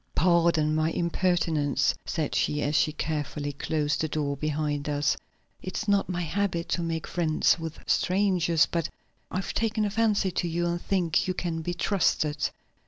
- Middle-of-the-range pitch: Yes, medium, 165 Hz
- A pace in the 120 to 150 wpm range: No, average, 165 wpm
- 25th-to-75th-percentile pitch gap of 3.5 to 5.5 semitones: No, average, 3.0 semitones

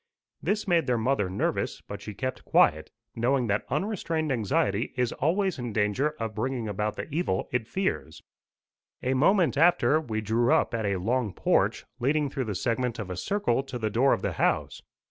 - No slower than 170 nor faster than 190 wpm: Yes, average, 185 wpm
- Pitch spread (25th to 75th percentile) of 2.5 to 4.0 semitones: No, wide, 5.6 semitones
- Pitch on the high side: No, low, 125 Hz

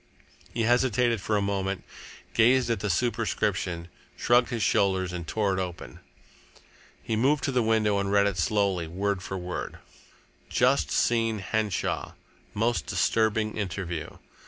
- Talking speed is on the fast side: No, average, 140 wpm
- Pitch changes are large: No, average, 3.3 semitones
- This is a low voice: Yes, low, 105 Hz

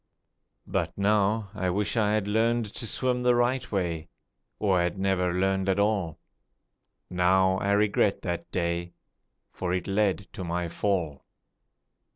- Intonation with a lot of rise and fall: No, average, 2.8 semitones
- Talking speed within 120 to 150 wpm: Yes, average, 145 wpm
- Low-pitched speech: Yes, very low, 95 Hz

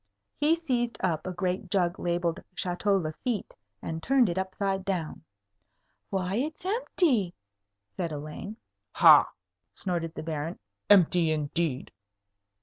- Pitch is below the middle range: No, medium, 185 Hz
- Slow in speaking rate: Yes, slow, 120 wpm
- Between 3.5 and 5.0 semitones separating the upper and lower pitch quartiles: Yes, average, 4.0 semitones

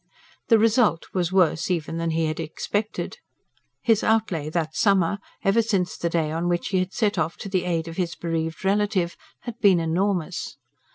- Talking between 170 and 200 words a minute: Yes, average, 180 wpm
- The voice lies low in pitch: No, medium, 180 Hz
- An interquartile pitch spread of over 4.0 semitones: No, average, 3.6 semitones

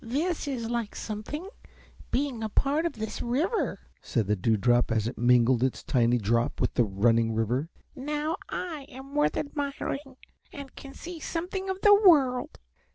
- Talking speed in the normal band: Yes, average, 160 wpm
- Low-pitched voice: No, very high, 250 Hz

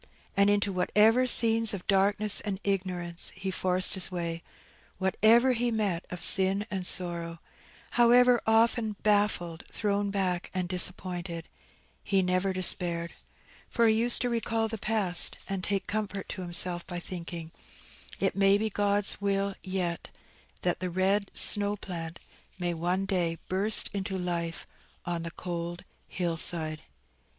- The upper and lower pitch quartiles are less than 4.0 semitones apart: Yes, average, 2.7 semitones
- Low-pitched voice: No, high, 190 Hz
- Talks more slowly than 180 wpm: Yes, average, 140 wpm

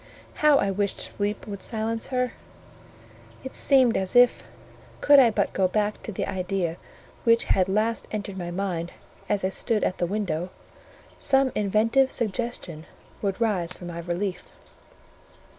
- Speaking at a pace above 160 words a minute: No, average, 150 wpm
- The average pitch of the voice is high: Yes, high, 205 Hz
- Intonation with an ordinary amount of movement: Yes, average, 3.8 semitones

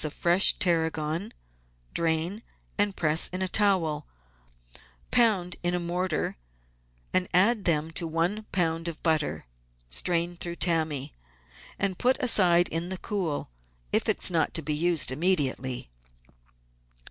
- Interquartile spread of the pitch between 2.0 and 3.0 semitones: Yes, average, 2.7 semitones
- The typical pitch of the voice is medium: Yes, medium, 170 Hz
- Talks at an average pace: No, slow, 130 wpm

